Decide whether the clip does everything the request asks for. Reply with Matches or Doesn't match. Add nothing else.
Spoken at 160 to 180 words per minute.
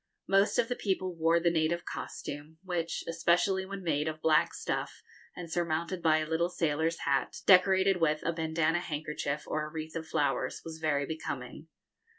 Matches